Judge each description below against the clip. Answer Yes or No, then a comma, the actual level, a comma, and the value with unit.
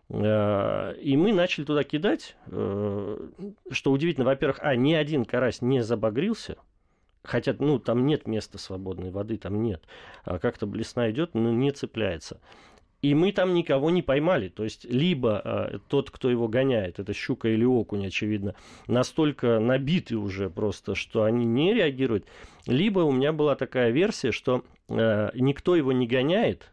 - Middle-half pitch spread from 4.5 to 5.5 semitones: Yes, average, 4.9 semitones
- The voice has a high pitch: No, low, 120 Hz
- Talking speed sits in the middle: Yes, average, 150 wpm